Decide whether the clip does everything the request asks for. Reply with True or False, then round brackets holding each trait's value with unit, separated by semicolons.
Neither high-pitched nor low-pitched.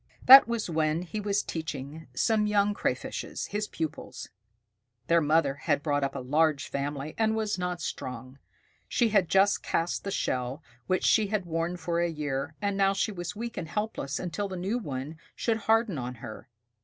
True (170 Hz)